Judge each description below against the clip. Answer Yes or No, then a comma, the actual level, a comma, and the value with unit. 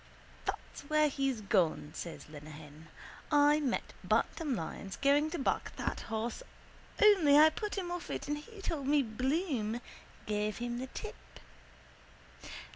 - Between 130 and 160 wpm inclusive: Yes, average, 140 wpm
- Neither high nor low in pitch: No, very high, 270 Hz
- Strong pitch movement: Yes, wide, 6.3 semitones